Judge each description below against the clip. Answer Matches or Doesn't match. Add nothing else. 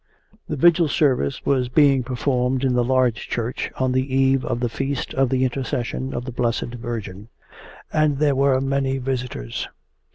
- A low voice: Matches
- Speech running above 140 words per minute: Matches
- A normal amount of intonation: Doesn't match